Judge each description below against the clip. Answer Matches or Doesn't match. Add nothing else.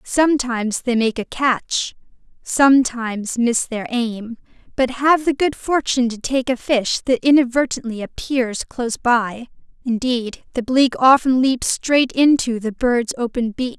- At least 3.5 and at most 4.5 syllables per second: Matches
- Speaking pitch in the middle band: Doesn't match